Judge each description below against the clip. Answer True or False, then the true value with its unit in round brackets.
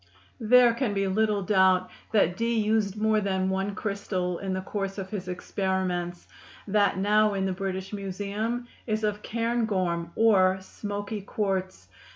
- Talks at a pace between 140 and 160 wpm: True (150 wpm)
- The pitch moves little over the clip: True (2.2 semitones)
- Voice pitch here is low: False (200 Hz)